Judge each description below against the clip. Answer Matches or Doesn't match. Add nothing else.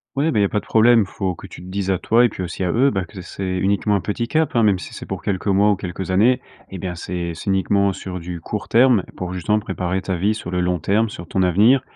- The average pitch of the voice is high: Doesn't match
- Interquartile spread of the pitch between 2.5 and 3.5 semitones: Matches